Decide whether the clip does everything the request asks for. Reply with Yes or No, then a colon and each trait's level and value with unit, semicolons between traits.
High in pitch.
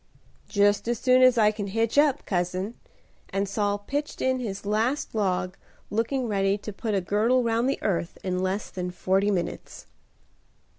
Yes: high, 205 Hz